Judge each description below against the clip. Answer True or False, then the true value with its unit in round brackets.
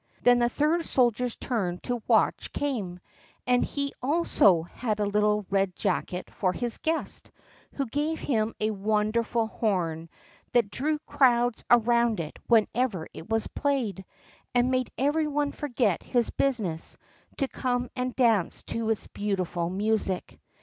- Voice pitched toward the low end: False (230 Hz)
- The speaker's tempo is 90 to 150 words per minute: True (140 wpm)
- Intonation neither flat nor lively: True (4.1 semitones)